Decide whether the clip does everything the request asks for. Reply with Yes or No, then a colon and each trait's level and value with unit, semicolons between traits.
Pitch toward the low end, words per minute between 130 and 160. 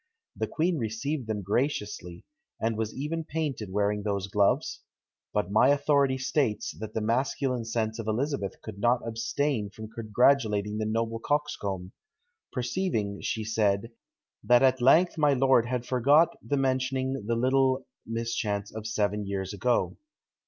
Yes: low, 115 Hz; average, 145 wpm